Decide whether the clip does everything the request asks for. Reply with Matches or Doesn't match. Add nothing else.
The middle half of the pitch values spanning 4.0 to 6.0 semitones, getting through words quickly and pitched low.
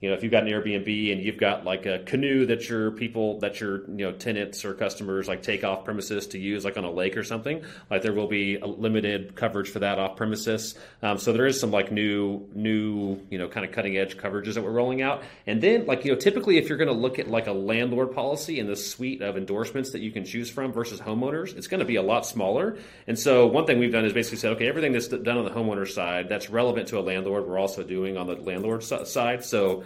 Doesn't match